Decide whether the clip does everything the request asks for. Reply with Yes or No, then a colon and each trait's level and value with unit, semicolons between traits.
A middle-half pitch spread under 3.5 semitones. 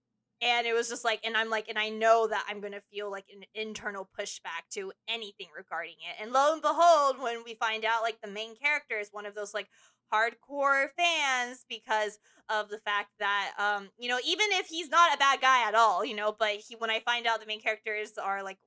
Yes: average, 2.9 semitones